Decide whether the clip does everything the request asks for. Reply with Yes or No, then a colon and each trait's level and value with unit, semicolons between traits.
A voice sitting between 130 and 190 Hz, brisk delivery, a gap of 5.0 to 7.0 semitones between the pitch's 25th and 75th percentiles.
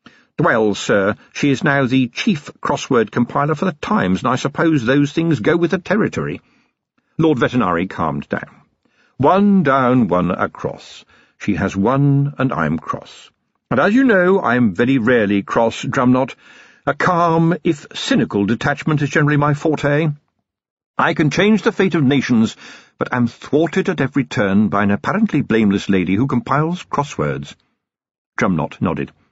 No: medium, 140 Hz; average, 155 wpm; wide, 5.4 semitones